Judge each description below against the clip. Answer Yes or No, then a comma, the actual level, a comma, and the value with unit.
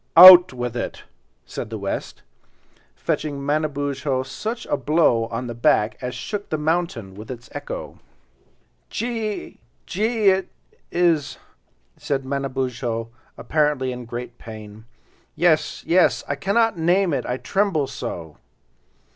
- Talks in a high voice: No, medium, 140 Hz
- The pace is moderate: No, slow, 130 wpm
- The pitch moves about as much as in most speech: No, wide, 6.4 semitones